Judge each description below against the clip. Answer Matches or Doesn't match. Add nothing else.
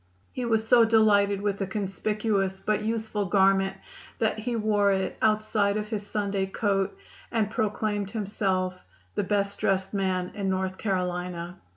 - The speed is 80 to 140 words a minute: Doesn't match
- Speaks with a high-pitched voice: Matches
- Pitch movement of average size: Doesn't match